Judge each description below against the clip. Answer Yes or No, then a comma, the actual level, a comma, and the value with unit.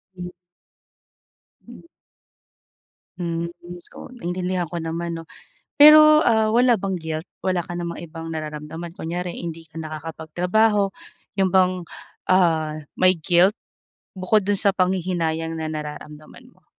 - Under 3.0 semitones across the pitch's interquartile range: Yes, narrow, 2.5 semitones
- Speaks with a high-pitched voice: No, medium, 175 Hz